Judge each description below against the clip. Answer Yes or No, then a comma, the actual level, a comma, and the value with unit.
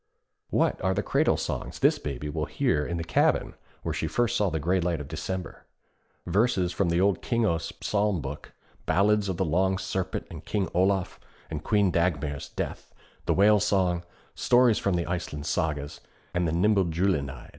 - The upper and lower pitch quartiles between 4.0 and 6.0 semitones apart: No, average, 3.6 semitones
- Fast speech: No, average, 175 wpm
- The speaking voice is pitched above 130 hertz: No, very low, 90 Hz